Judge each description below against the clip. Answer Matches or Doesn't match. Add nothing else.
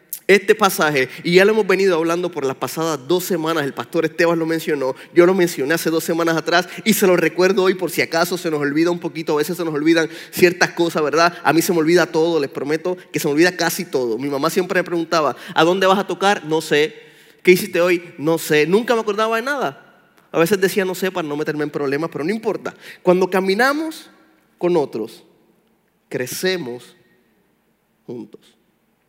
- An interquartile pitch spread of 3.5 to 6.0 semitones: Doesn't match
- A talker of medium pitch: Matches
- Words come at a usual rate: Doesn't match